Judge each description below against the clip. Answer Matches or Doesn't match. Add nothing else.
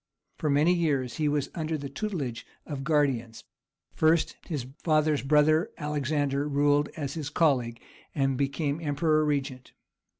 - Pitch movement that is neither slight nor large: Doesn't match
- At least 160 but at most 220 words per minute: Doesn't match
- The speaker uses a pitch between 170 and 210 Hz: Doesn't match